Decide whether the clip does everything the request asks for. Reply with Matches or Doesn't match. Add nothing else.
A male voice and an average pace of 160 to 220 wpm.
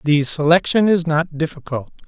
Doesn't match